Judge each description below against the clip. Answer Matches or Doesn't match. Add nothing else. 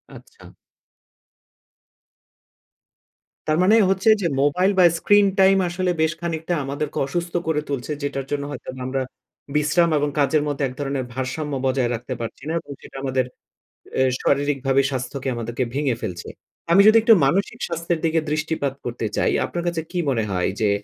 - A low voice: Doesn't match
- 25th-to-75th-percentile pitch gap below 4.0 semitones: Doesn't match